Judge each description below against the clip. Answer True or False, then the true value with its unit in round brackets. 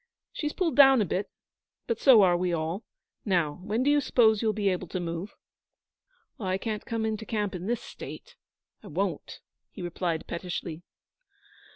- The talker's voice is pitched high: True (200 Hz)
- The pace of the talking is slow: False (170 wpm)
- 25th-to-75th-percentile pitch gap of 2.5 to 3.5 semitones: False (4.3 semitones)